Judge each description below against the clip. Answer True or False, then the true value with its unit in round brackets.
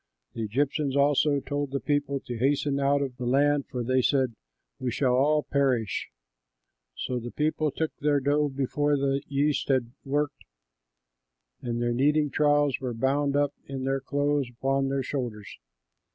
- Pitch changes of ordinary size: False (2.0 semitones)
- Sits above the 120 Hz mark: True (140 Hz)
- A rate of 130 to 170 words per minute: True (160 wpm)